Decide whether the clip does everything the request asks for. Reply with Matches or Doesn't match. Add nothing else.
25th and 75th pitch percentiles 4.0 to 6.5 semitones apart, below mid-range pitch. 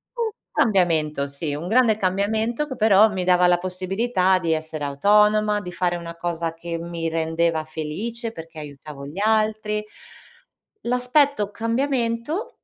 Doesn't match